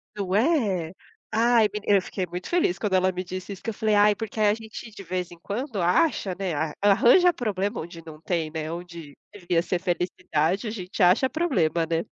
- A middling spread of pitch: Yes, average, 3.7 semitones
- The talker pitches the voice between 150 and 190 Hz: Yes, medium, 185 Hz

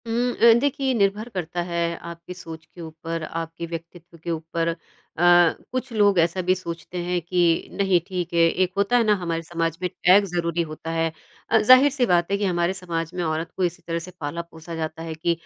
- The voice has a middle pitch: Yes, medium, 175 Hz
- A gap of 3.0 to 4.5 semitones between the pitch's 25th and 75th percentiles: No, narrow, 2.4 semitones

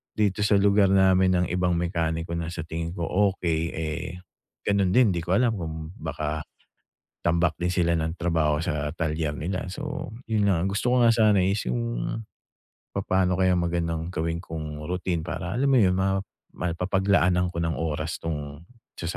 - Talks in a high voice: No, very low, 85 Hz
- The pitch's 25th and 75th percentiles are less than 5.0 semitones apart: Yes, average, 2.8 semitones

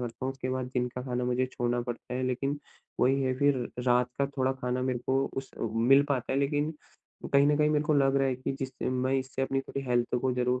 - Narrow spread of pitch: Yes, narrow, 1.6 semitones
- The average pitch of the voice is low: Yes, low, 130 Hz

